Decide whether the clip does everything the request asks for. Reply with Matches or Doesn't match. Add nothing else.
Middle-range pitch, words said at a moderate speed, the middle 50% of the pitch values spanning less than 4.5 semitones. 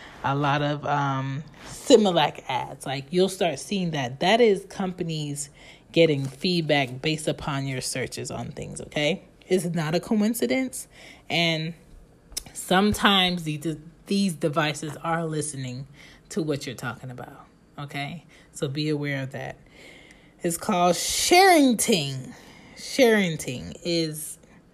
Doesn't match